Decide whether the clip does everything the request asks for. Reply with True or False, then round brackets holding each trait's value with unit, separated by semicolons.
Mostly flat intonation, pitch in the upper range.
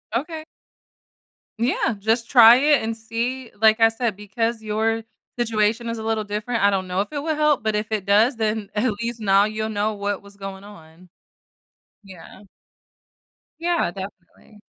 True (2.3 semitones; 220 Hz)